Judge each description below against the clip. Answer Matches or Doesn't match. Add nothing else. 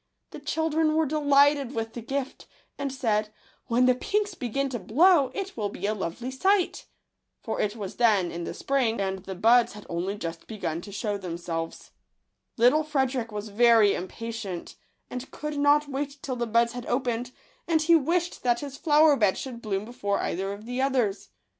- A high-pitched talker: Matches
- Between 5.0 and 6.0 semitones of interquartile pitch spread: Matches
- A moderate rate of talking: Matches